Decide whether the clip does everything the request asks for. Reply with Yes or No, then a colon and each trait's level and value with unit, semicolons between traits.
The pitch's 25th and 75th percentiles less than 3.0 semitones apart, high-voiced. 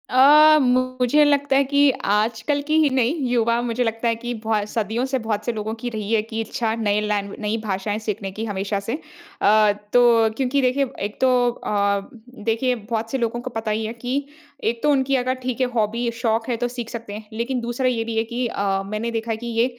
Yes: narrow, 2.6 semitones; high, 230 Hz